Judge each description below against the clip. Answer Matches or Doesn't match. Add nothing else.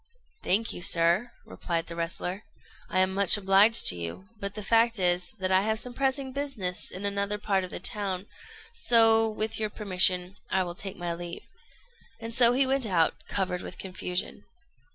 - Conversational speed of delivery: Matches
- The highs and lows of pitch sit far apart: Doesn't match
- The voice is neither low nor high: Doesn't match